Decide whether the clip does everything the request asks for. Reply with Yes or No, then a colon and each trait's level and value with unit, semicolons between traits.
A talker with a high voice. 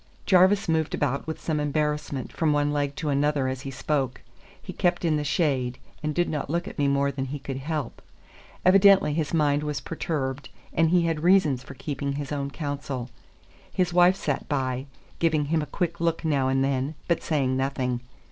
No: medium, 145 Hz